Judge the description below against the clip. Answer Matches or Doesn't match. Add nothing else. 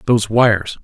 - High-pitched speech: Doesn't match